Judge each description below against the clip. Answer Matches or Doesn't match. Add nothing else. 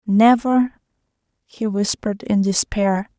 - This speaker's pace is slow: Matches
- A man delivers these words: Doesn't match